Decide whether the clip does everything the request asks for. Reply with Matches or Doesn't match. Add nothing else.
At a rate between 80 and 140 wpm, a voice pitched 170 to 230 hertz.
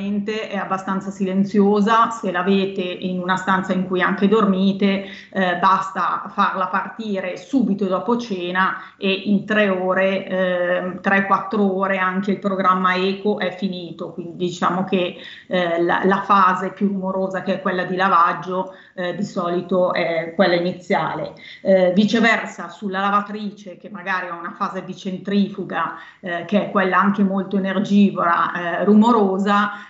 Doesn't match